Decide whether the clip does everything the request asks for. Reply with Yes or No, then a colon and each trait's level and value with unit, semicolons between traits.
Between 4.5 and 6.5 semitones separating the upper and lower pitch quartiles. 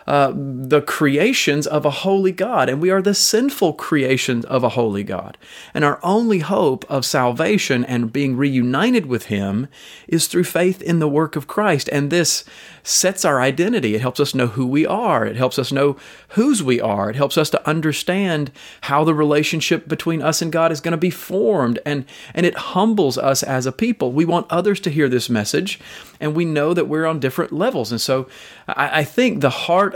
Yes: average, 4.9 semitones